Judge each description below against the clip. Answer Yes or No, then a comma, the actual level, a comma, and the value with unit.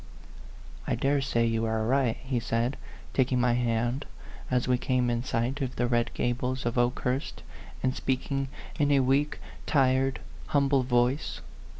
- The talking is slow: No, average, 160 wpm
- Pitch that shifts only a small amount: Yes, narrow, 2.0 semitones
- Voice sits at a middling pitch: No, low, 125 Hz